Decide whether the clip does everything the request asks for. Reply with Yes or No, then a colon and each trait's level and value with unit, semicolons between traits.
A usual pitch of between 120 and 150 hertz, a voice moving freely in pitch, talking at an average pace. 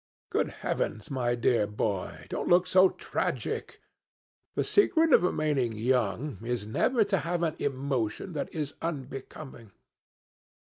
No: low, 135 Hz; wide, 6.6 semitones; slow, 130 wpm